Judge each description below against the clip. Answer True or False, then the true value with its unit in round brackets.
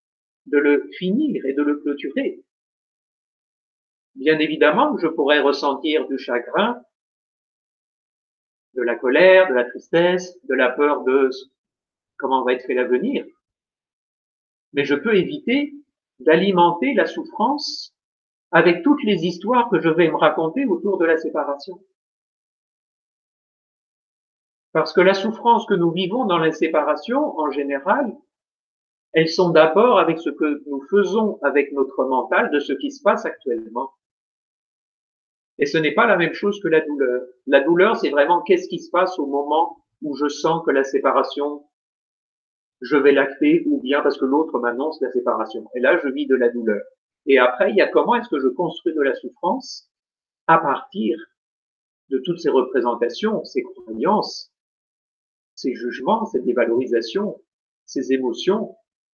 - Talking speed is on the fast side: False (150 wpm)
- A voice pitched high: False (165 Hz)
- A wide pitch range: True (6.5 semitones)